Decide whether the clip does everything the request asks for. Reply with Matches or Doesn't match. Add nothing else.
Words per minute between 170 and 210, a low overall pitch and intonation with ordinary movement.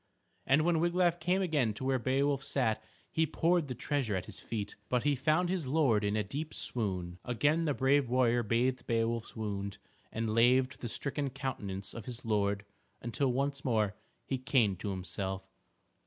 Matches